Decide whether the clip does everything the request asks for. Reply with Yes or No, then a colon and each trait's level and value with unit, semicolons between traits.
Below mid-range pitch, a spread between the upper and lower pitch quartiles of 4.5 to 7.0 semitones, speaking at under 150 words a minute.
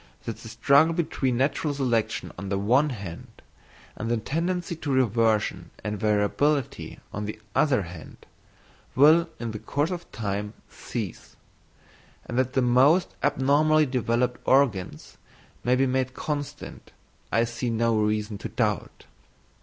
Yes: low, 125 Hz; average, 4.9 semitones; average, 140 wpm